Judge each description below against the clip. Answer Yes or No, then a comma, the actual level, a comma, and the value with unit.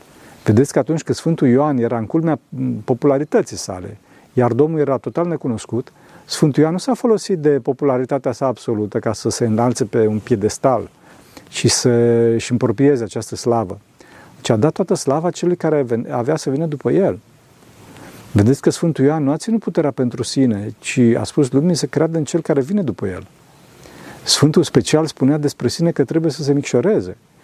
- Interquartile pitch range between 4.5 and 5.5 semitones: Yes, average, 4.9 semitones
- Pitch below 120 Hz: No, low, 135 Hz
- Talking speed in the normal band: No, fast, 180 wpm